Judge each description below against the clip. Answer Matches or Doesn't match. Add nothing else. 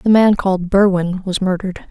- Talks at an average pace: Matches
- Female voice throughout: Matches